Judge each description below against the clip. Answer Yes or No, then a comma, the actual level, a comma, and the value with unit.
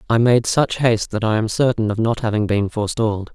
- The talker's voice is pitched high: No, low, 110 Hz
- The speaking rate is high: Yes, fast, 235 wpm